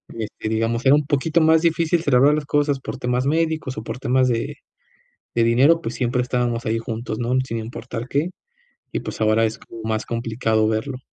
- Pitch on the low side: Yes, low, 125 Hz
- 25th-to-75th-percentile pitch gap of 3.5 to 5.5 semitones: Yes, average, 4.0 semitones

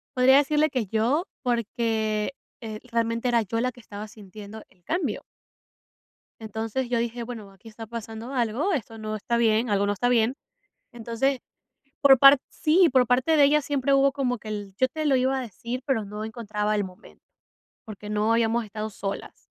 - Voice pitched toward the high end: Yes, high, 230 Hz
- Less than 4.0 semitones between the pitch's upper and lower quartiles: Yes, average, 3.2 semitones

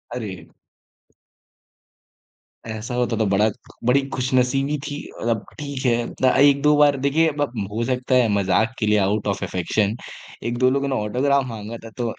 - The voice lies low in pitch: Yes, low, 125 Hz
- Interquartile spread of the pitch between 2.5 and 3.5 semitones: No, average, 4.2 semitones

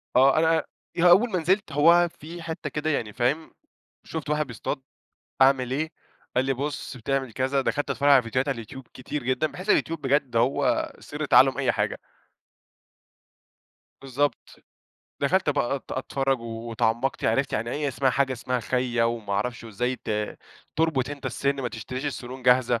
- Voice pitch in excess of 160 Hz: No, low, 135 Hz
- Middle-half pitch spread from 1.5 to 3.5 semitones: Yes, average, 3.2 semitones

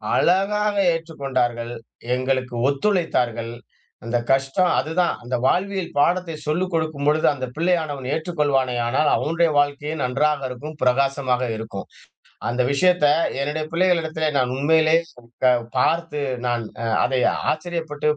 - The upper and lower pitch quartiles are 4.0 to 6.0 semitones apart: Yes, average, 4.4 semitones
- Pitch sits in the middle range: Yes, medium, 150 Hz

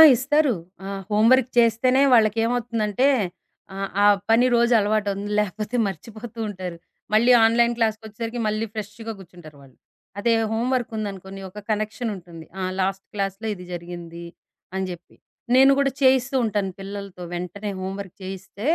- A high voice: Yes, high, 210 Hz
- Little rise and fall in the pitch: No, average, 3.3 semitones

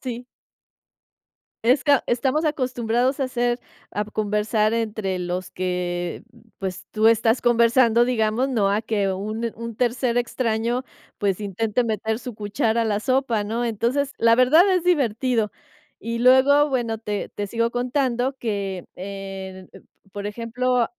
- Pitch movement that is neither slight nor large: Yes, average, 3.2 semitones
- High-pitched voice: Yes, high, 230 Hz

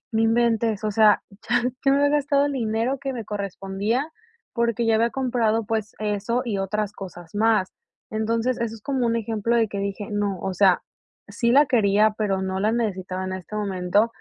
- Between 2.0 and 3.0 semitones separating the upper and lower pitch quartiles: Yes, average, 2.7 semitones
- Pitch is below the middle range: No, high, 220 Hz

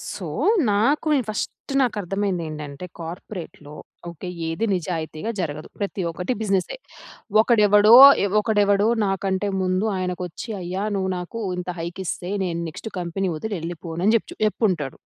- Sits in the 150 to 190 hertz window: Yes, medium, 185 Hz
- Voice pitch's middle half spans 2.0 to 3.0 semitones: No, average, 3.4 semitones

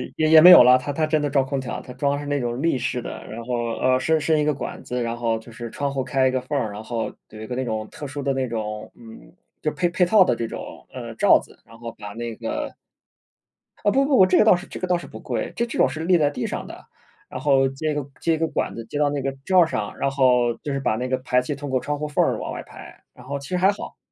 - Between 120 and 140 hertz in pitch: Yes, low, 135 Hz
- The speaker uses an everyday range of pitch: Yes, average, 4.3 semitones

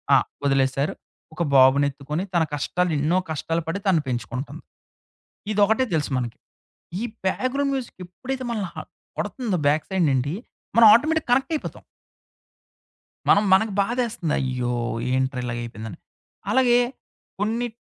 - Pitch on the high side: No, medium, 170 Hz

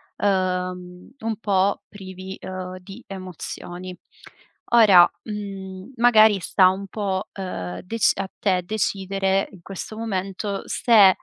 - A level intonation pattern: Yes, narrow, 1.7 semitones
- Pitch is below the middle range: No, high, 190 Hz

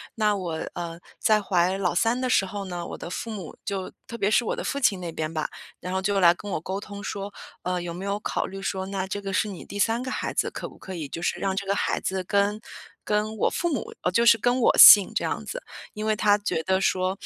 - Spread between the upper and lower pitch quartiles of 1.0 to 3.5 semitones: Yes, narrow, 2.5 semitones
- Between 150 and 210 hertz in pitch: Yes, high, 195 Hz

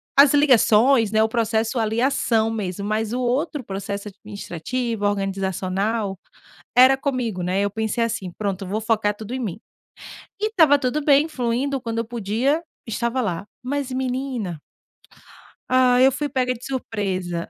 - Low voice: No, high, 230 Hz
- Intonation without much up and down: No, average, 4.1 semitones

